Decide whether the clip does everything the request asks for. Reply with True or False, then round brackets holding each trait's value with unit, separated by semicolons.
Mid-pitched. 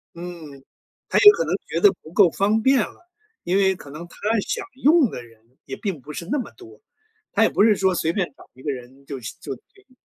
True (180 Hz)